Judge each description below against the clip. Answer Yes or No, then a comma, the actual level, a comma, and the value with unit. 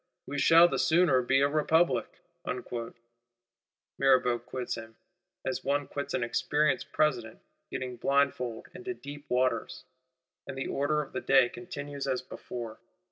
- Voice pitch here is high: No, low, 135 Hz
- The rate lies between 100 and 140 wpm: Yes, slow, 135 wpm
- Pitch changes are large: No, average, 2.7 semitones